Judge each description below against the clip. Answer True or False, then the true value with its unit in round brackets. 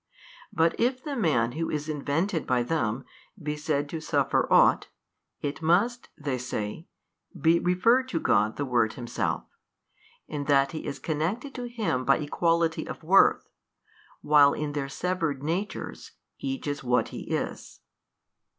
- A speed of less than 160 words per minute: True (150 wpm)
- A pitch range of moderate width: True (4.5 semitones)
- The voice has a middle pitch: True (155 Hz)